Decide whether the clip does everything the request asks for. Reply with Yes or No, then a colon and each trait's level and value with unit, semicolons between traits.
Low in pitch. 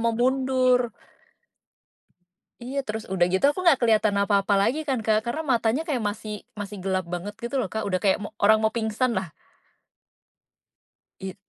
No: high, 220 Hz